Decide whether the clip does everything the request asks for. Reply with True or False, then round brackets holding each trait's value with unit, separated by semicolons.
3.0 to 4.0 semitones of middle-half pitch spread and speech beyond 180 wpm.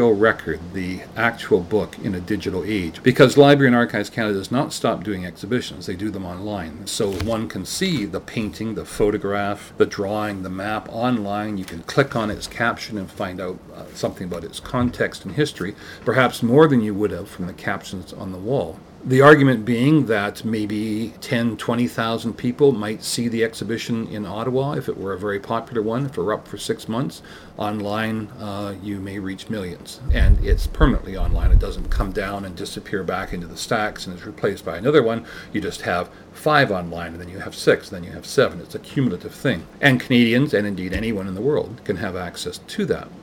True (3.7 semitones; 205 wpm)